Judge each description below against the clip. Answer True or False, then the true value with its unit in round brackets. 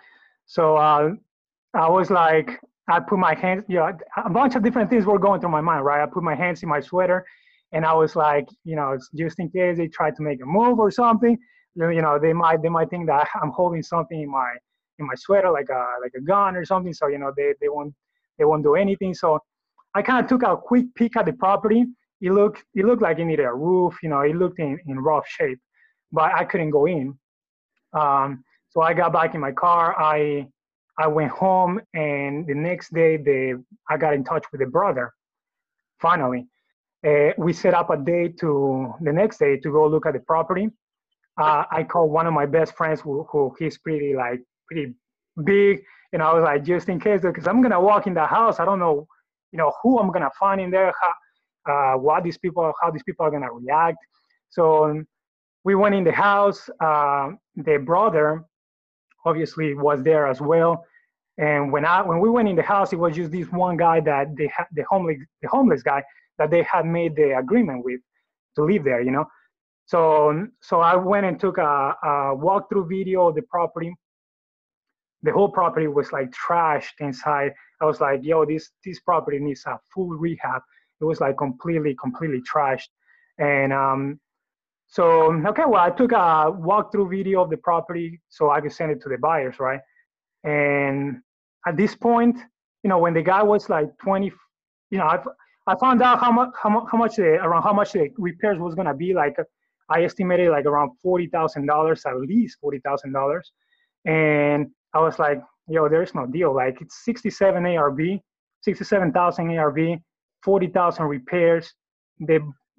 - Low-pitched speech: False (165 Hz)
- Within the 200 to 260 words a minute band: True (205 wpm)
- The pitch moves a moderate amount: True (4.8 semitones)